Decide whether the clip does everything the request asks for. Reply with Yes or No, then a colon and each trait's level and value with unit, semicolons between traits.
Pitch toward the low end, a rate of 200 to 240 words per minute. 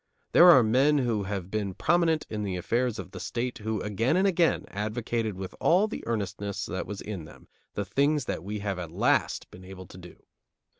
Yes: low, 105 Hz; fast, 205 wpm